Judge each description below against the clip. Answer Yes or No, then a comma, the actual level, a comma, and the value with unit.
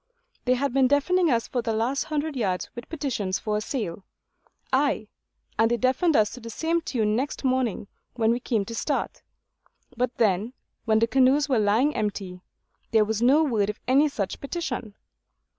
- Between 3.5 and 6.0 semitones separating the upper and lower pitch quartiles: Yes, average, 4.2 semitones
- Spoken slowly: No, average, 180 wpm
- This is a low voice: No, high, 240 Hz